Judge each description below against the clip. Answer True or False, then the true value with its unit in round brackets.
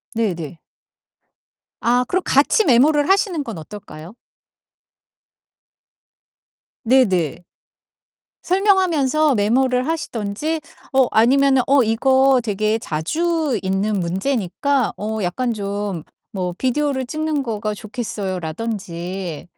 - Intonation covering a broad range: True (6.1 semitones)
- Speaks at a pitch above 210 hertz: True (230 Hz)